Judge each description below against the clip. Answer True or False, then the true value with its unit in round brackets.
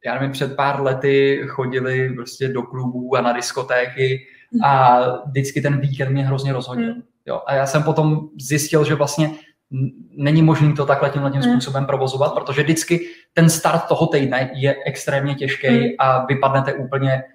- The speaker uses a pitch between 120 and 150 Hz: True (140 Hz)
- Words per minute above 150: True (165 wpm)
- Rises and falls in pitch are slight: True (2.2 semitones)